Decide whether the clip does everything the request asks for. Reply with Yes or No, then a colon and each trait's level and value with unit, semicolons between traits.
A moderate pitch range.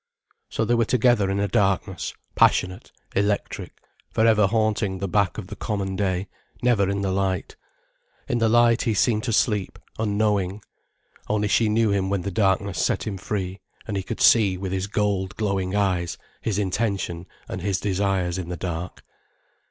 No: narrow, 2.2 semitones